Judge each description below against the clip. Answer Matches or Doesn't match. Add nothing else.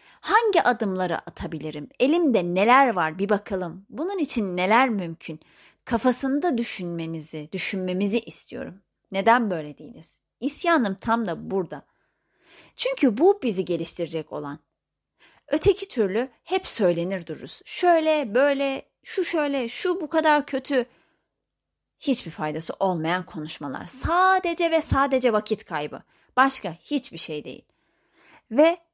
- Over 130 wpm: Doesn't match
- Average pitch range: Doesn't match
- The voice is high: Matches